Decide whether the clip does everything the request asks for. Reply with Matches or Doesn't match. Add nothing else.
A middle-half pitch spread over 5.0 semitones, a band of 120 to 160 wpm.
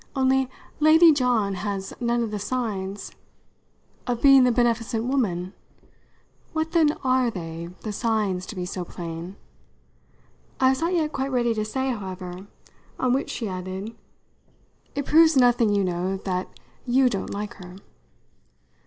Matches